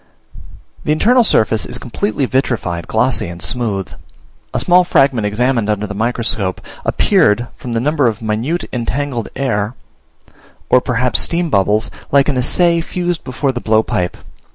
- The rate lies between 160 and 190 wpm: No, average, 145 wpm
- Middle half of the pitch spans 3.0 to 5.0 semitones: Yes, average, 4.7 semitones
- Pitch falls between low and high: No, low, 120 Hz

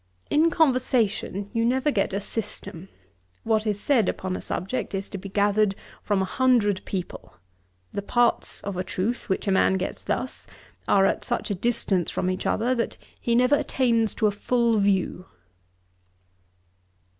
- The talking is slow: No, average, 165 wpm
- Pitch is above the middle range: Yes, high, 210 Hz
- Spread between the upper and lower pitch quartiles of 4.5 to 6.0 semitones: No, average, 3.7 semitones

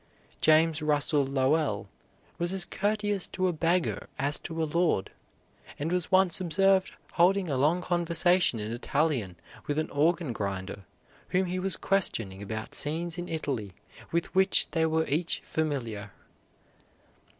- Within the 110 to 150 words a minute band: Yes, average, 140 wpm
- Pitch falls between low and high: Yes, medium, 160 Hz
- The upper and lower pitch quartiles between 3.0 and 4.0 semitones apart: No, average, 4.6 semitones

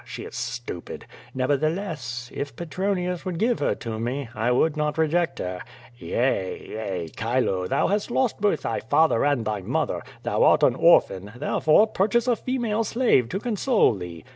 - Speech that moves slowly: No, average, 165 wpm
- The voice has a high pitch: No, medium, 145 Hz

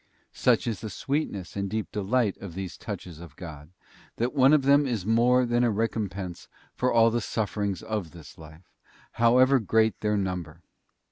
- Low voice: Yes, low, 105 Hz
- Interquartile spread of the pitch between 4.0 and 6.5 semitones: Yes, average, 4.5 semitones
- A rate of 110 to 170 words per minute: No, average, 180 wpm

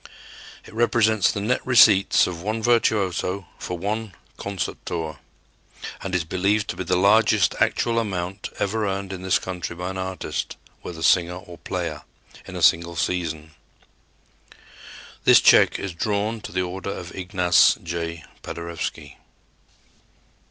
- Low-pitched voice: Yes, very low, 95 Hz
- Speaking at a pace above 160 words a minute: No, average, 140 wpm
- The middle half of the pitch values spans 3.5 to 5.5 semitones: No, average, 3.0 semitones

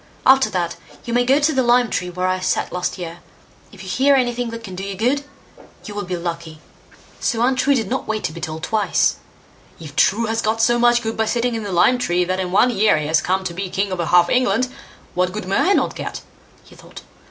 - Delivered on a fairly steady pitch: No, average, 5.1 semitones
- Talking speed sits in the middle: No, fast, 245 wpm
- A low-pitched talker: No, high, 205 Hz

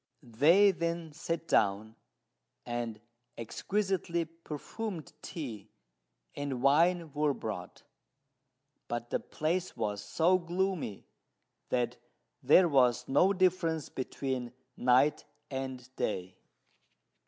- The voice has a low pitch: No, medium, 145 Hz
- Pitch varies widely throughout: Yes, wide, 5.8 semitones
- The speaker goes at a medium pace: No, slow, 95 wpm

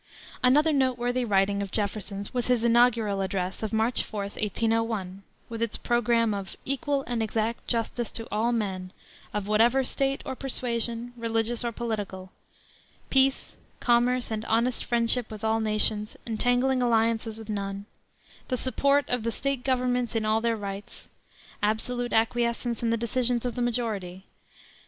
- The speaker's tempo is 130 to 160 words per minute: Yes, average, 150 wpm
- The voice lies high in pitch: Yes, high, 230 Hz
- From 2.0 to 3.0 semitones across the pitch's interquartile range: Yes, narrow, 2.5 semitones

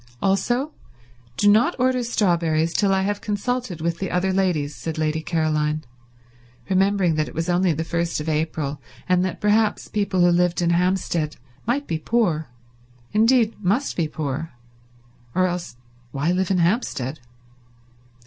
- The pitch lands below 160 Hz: No, medium, 180 Hz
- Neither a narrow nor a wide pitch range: Yes, average, 4.3 semitones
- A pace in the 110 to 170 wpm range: Yes, average, 150 wpm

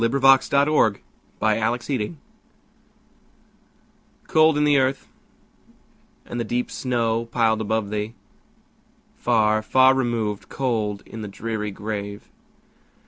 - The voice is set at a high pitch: No, low, 115 Hz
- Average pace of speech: No, slow, 100 wpm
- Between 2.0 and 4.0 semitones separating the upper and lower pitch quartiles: Yes, average, 3.5 semitones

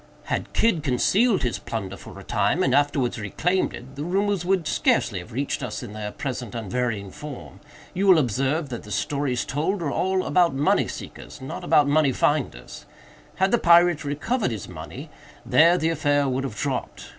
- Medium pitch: Yes, medium, 145 Hz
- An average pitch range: No, wide, 6.0 semitones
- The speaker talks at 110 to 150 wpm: No, average, 180 wpm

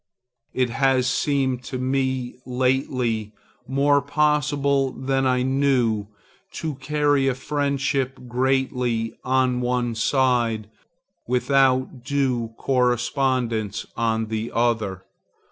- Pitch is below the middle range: Yes, low, 130 Hz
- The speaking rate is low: Yes, slow, 95 wpm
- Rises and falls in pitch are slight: Yes, narrow, 2.1 semitones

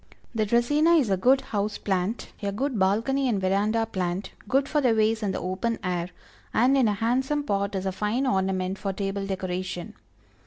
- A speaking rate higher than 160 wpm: Yes, average, 190 wpm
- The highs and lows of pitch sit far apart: No, average, 4.2 semitones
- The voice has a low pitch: No, high, 210 Hz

